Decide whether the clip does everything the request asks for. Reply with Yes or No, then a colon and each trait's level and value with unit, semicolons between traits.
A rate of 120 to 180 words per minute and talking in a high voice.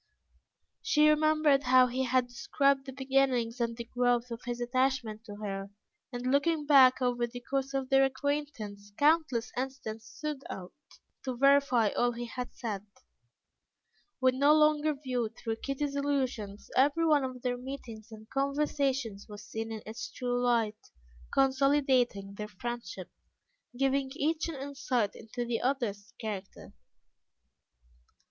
Yes: average, 140 wpm; very high, 255 Hz